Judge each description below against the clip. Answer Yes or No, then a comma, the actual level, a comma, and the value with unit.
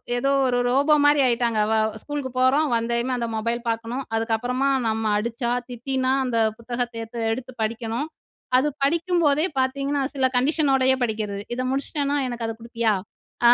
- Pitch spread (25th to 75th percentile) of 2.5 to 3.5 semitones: Yes, average, 3.0 semitones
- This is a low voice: No, very high, 250 Hz